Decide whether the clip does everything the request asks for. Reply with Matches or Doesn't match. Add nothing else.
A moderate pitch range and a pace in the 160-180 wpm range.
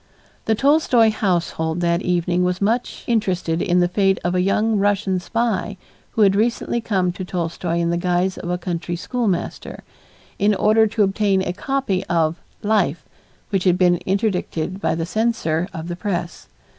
Matches